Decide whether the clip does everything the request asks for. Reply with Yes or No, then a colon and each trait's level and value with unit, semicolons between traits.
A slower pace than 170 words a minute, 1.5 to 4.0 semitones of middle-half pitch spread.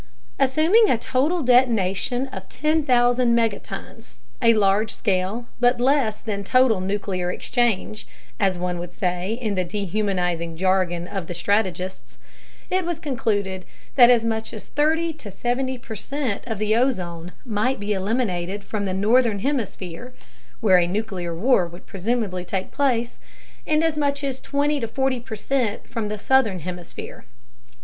No: average, 140 wpm; average, 5.2 semitones